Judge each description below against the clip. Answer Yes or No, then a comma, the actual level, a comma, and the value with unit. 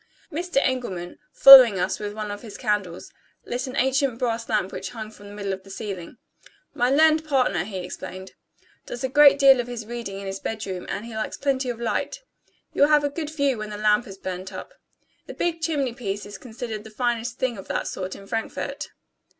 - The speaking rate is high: Yes, fast, 215 wpm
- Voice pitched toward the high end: Yes, high, 230 Hz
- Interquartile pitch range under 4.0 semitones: No, average, 4.7 semitones